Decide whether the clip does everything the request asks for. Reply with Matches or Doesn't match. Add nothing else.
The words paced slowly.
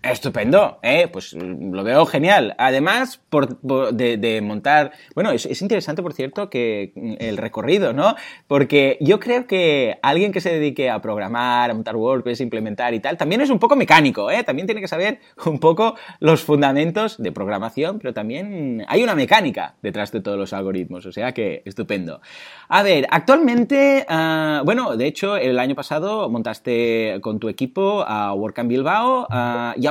Doesn't match